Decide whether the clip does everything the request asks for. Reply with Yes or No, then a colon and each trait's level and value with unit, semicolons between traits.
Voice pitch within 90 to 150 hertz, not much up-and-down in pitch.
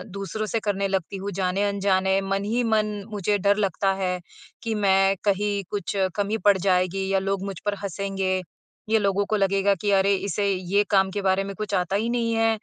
No: high, 200 Hz; narrow, 1.2 semitones